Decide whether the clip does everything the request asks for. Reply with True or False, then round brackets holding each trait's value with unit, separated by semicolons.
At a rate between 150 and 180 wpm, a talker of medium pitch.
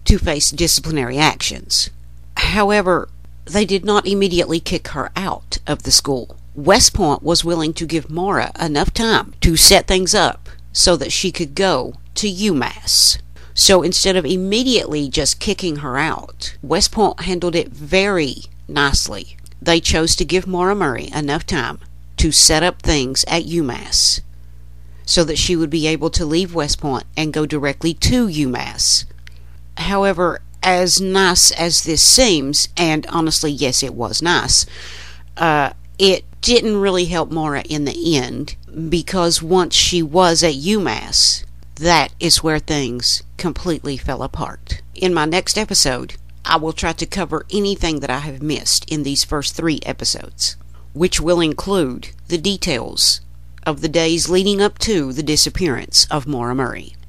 True (155 wpm; 155 Hz)